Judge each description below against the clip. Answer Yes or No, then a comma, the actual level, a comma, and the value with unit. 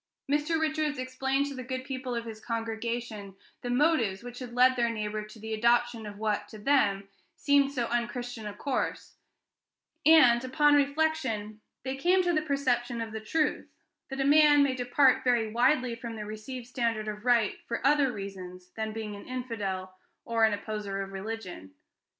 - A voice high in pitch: Yes, high, 240 Hz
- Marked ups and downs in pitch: No, average, 3.9 semitones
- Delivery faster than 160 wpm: Yes, average, 175 wpm